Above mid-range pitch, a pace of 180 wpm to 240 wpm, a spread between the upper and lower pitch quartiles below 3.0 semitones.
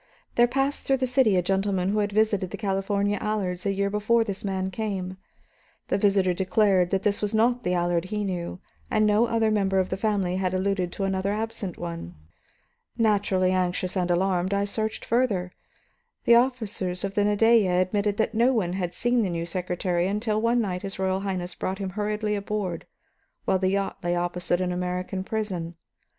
Yes: high, 195 Hz; average, 190 wpm; narrow, 2.6 semitones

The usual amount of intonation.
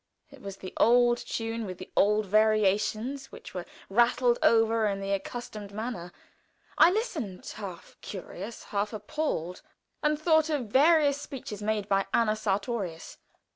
Yes: average, 3.9 semitones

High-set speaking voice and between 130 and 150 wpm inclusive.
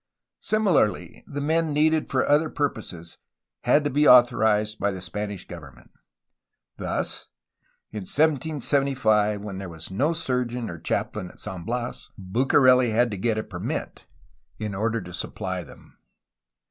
No: low, 115 Hz; average, 140 wpm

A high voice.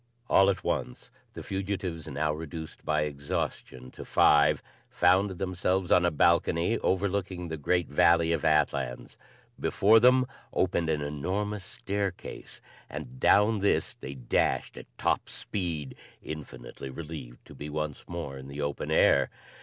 No: very low, 80 Hz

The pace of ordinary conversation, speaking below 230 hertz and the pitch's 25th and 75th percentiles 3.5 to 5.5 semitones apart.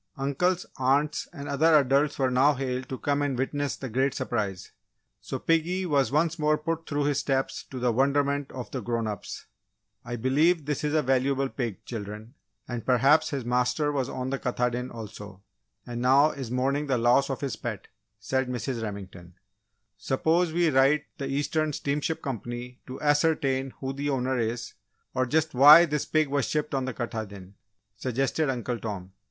No: average, 175 wpm; low, 135 Hz; average, 3.1 semitones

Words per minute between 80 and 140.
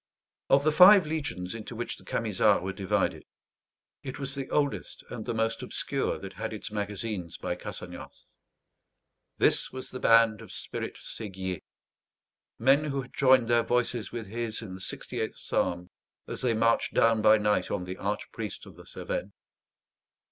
No: average, 160 wpm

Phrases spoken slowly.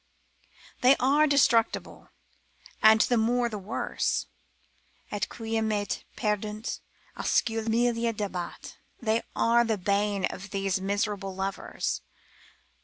Yes: slow, 105 wpm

